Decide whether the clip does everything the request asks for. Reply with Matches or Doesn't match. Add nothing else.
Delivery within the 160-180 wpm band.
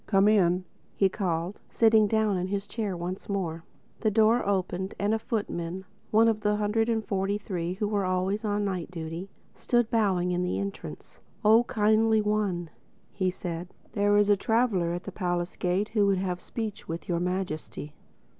Matches